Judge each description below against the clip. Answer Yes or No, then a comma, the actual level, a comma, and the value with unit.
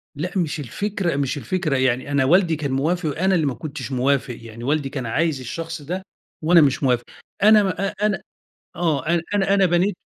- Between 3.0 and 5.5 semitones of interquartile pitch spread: Yes, average, 4.9 semitones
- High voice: No, medium, 155 Hz